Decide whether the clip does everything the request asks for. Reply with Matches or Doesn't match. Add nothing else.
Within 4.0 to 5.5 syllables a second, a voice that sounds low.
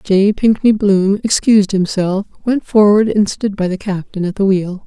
Doesn't match